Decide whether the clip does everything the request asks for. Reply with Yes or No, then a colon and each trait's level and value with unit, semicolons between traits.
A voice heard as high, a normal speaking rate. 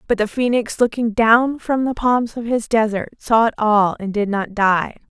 No: high, 225 Hz; fast, 210 wpm